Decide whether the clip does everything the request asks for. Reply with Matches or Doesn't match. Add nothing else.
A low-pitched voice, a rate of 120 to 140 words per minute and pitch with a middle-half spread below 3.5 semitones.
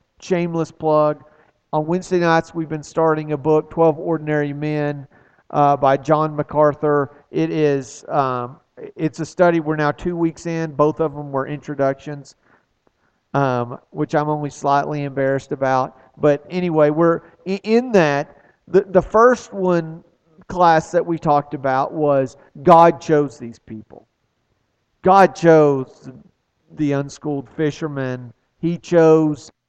Doesn't match